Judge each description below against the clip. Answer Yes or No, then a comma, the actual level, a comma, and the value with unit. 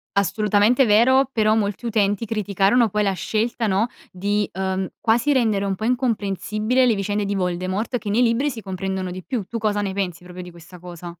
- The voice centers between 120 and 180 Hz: No, high, 205 Hz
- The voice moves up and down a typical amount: Yes, average, 3.2 semitones